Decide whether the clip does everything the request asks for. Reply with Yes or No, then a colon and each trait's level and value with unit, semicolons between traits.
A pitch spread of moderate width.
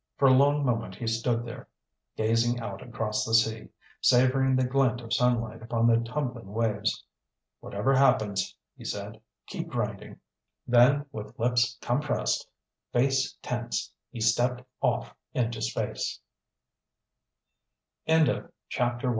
No: narrow, 2.3 semitones